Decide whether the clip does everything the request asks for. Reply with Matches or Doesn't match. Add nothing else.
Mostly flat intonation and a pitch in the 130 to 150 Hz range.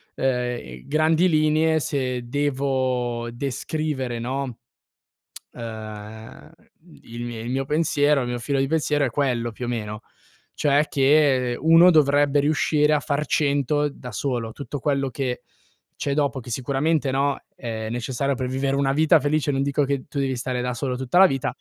Doesn't match